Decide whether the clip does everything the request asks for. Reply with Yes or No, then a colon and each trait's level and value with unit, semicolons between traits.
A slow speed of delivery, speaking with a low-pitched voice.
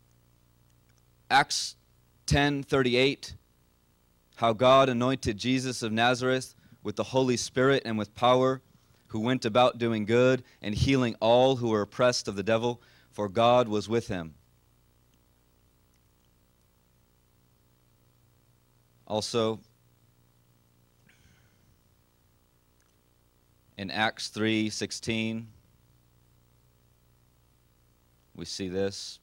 Yes: slow, 85 wpm; low, 100 Hz